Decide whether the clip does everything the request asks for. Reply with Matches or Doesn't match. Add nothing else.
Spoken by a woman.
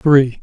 Doesn't match